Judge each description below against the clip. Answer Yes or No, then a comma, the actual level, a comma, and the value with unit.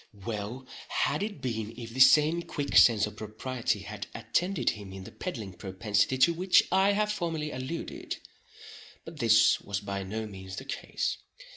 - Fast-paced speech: No, average, 160 wpm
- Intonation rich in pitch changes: Yes, wide, 7.2 semitones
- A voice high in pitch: No, low, 120 Hz